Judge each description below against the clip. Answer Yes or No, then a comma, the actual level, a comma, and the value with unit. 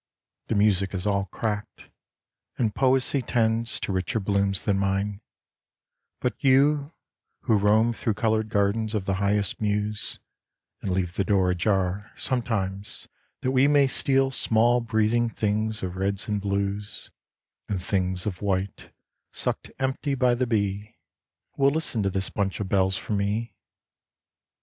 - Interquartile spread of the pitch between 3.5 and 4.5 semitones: No, average, 3.0 semitones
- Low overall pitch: Yes, low, 105 Hz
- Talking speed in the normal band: Yes, average, 145 wpm